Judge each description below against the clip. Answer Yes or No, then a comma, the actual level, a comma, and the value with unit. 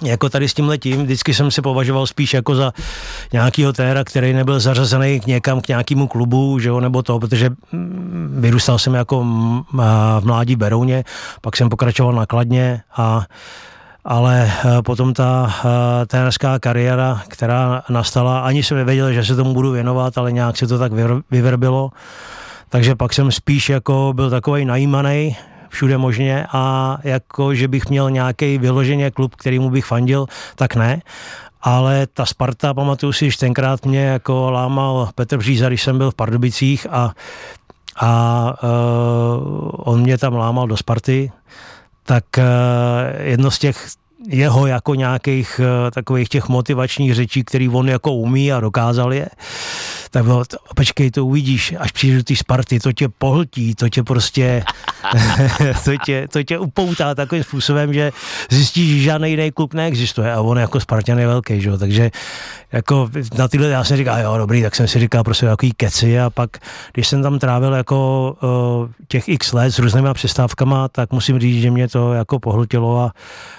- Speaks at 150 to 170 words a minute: Yes, average, 165 wpm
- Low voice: Yes, low, 130 Hz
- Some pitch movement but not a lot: No, narrow, 2.0 semitones